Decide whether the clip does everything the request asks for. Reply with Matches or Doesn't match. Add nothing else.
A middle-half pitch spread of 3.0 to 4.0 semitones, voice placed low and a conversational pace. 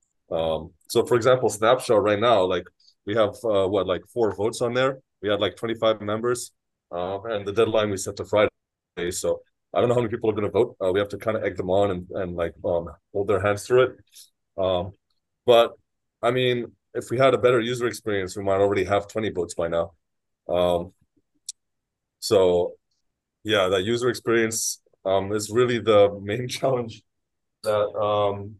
Matches